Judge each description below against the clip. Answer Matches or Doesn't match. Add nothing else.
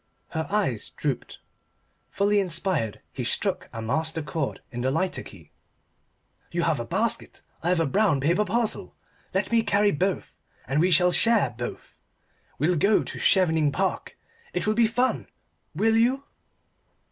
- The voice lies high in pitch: Doesn't match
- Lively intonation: Matches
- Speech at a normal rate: Matches